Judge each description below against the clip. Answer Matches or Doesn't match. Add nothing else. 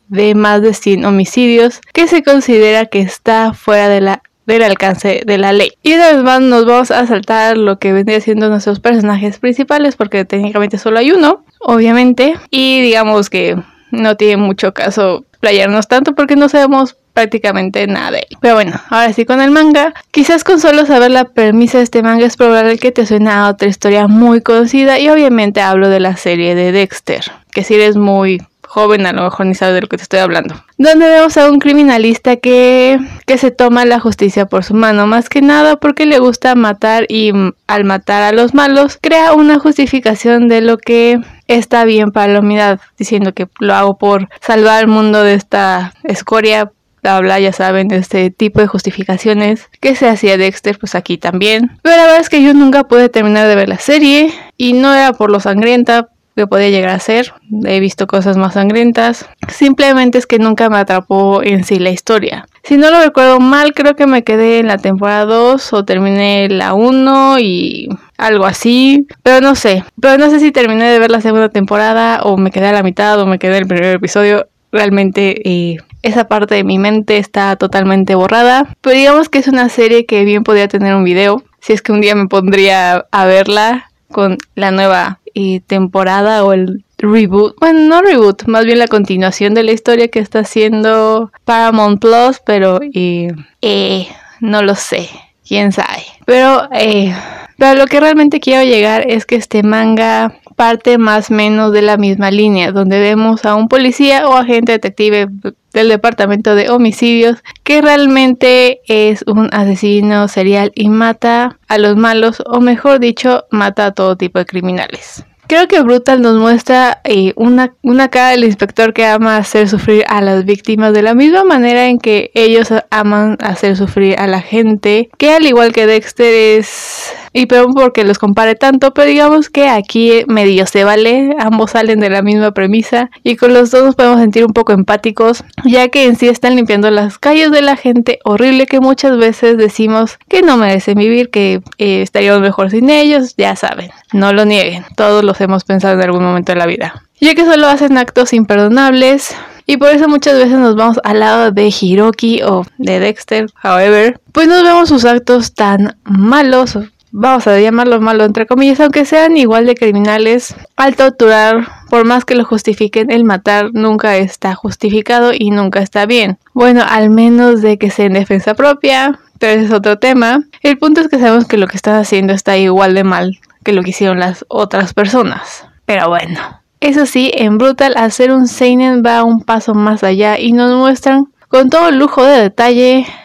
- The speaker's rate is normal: Doesn't match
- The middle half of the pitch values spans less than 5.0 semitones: Matches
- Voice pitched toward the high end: Matches